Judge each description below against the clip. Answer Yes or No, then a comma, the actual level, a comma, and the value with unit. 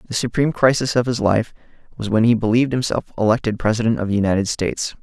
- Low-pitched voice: Yes, low, 115 Hz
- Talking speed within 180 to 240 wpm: Yes, fast, 205 wpm